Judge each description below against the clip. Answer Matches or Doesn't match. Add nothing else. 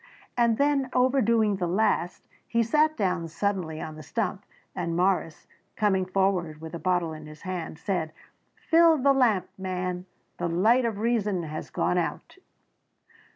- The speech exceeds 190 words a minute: Doesn't match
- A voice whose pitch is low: Doesn't match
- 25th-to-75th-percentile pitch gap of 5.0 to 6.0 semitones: Matches